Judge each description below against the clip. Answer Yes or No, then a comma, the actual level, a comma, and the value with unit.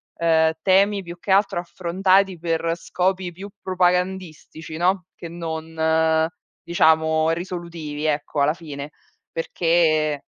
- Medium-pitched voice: Yes, medium, 170 Hz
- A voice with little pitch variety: Yes, narrow, 2.3 semitones